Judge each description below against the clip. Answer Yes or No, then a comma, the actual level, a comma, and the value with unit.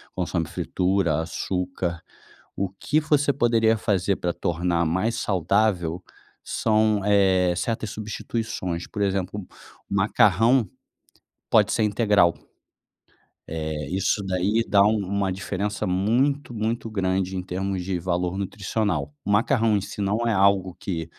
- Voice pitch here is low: Yes, low, 100 Hz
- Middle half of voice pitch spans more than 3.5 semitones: No, average, 3.1 semitones